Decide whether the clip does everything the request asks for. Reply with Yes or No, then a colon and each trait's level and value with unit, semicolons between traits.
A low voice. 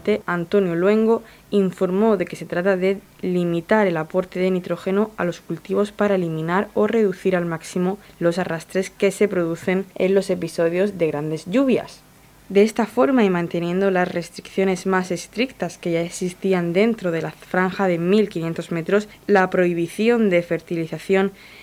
No: medium, 185 Hz